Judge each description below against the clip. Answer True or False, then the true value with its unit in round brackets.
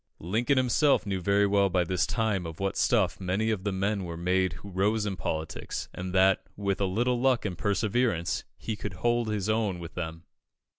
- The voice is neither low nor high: False (100 Hz)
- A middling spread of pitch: True (3.2 semitones)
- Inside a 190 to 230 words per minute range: True (200 wpm)